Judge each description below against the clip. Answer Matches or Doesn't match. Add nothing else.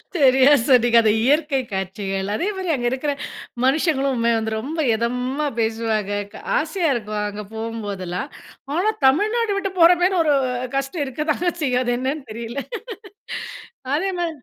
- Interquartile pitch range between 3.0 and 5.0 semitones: Doesn't match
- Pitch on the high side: Matches